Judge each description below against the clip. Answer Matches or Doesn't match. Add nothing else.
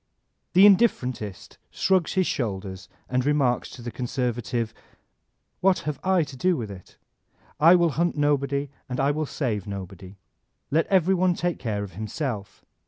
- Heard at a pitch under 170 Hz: Matches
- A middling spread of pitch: Doesn't match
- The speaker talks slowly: Doesn't match